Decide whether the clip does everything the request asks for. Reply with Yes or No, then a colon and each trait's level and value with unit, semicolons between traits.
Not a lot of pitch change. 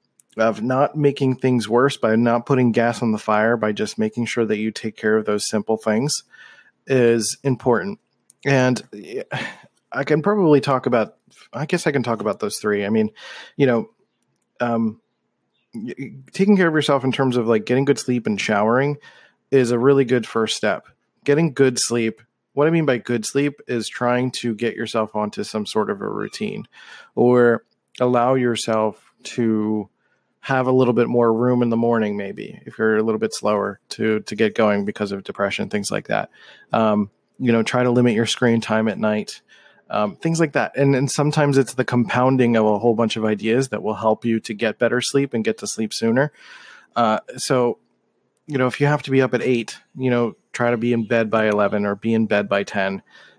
No: average, 3.3 semitones